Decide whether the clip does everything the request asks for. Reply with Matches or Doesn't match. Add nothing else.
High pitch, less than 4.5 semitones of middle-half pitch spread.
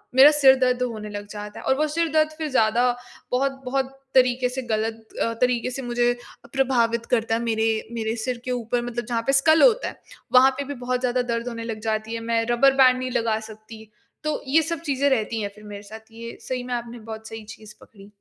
Matches